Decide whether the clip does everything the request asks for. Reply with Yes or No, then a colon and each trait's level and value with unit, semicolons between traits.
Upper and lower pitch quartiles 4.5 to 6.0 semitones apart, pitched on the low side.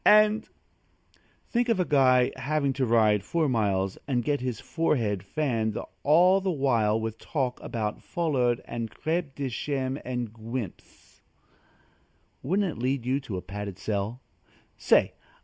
Yes: average, 5.2 semitones; low, 130 Hz